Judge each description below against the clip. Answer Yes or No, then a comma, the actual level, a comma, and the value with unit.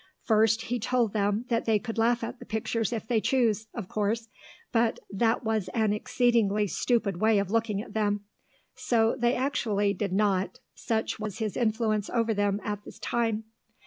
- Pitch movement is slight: Yes, narrow, 1.9 semitones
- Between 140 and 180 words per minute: Yes, average, 175 wpm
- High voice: Yes, high, 220 Hz